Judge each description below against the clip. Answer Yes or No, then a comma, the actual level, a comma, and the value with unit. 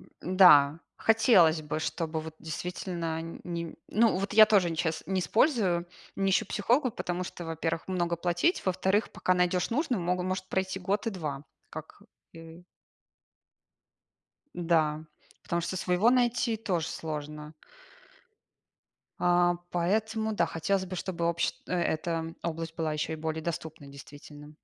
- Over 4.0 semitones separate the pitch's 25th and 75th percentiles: No, average, 2.9 semitones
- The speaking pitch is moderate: Yes, medium, 175 Hz